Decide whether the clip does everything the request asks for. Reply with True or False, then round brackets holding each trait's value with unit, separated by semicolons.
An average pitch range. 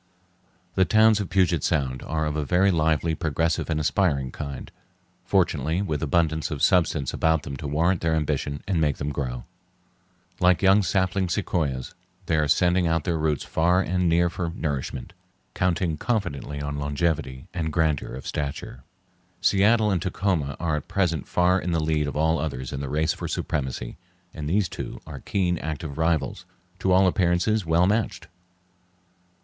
True (3.6 semitones)